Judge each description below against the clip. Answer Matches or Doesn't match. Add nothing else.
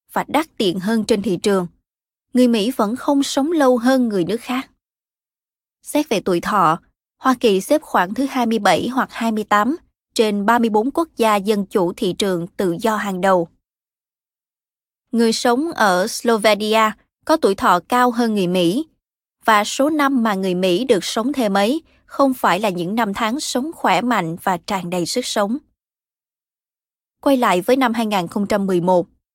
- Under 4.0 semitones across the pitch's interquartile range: Doesn't match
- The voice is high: Matches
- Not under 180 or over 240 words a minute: Doesn't match